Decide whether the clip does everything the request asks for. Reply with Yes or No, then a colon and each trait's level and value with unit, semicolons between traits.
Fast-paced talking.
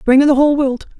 Yes: fast, 300 wpm